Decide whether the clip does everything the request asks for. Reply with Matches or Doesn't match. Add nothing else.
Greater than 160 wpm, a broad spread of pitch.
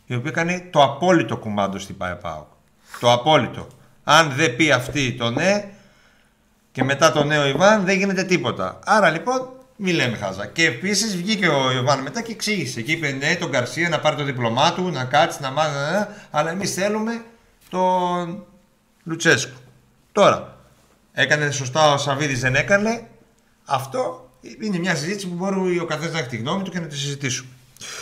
Matches